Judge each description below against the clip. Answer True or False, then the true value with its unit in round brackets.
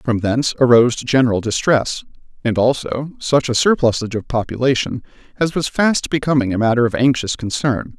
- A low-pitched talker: True (125 Hz)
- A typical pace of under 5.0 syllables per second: False (5.5 syllables/s)